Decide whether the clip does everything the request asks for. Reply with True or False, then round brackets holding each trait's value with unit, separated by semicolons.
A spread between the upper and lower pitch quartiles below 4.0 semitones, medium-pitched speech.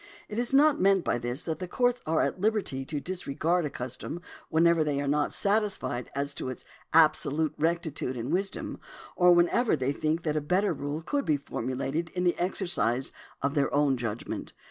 False (4.6 semitones; 155 Hz)